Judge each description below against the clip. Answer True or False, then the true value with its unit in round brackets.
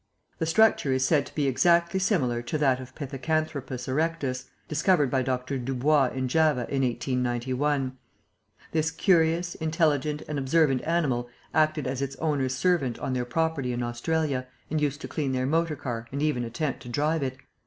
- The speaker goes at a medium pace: True (170 wpm)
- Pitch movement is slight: False (3.7 semitones)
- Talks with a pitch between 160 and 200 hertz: False (140 Hz)